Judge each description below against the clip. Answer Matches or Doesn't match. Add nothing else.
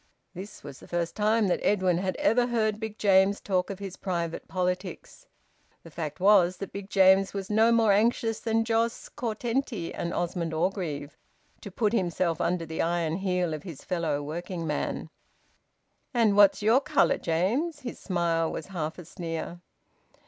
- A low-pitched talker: Doesn't match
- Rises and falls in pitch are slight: Doesn't match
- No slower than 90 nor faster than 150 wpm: Doesn't match